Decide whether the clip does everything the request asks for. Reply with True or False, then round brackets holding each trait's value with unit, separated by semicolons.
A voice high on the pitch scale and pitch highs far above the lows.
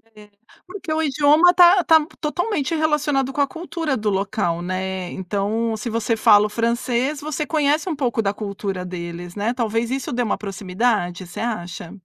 True (230 Hz; 7.0 semitones)